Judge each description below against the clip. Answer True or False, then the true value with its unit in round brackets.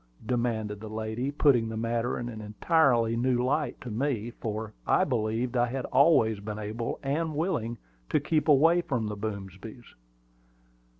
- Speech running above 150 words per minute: True (160 wpm)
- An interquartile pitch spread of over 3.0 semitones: True (3.7 semitones)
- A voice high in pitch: False (120 Hz)